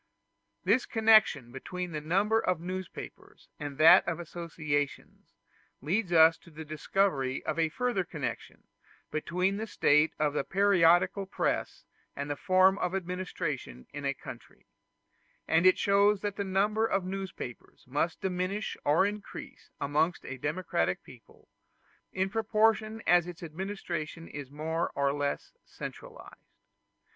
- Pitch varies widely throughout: No, average, 4.4 semitones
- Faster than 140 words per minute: No, slow, 135 wpm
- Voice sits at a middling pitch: Yes, medium, 175 Hz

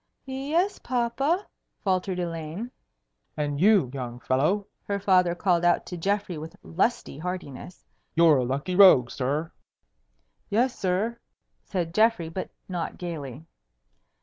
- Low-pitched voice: No, medium, 180 Hz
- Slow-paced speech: Yes, slow, 125 wpm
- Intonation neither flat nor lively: Yes, average, 4.9 semitones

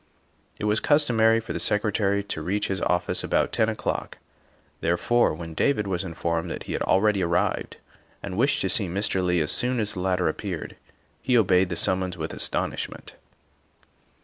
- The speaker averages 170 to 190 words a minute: Yes, average, 175 wpm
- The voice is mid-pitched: No, very low, 95 Hz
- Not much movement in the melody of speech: No, average, 3.4 semitones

